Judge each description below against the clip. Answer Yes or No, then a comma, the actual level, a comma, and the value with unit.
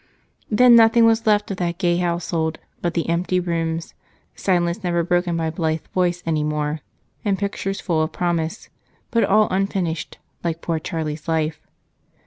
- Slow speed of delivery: No, average, 155 wpm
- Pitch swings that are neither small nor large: Yes, average, 3.0 semitones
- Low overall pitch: No, medium, 175 Hz